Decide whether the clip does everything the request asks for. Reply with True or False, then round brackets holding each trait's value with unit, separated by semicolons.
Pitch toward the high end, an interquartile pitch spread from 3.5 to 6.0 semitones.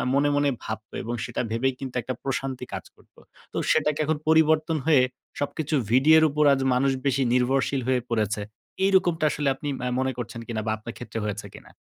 False (135 Hz; 3.8 semitones)